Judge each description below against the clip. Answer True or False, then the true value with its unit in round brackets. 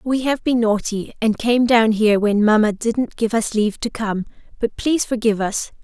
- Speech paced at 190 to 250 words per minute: True (205 wpm)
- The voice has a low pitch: False (225 Hz)